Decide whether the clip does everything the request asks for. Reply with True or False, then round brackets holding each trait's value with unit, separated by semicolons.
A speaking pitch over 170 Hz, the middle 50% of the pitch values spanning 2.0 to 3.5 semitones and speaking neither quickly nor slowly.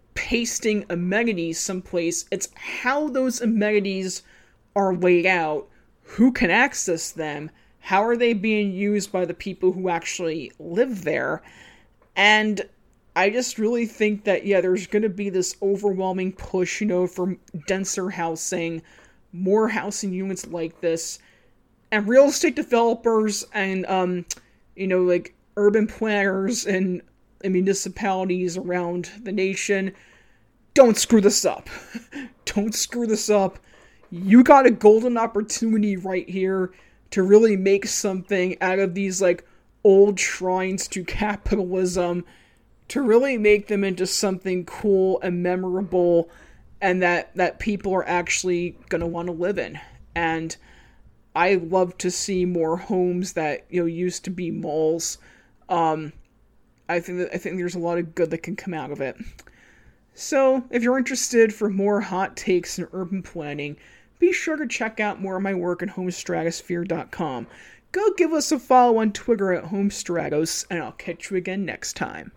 True (190 Hz; 3.1 semitones; 150 wpm)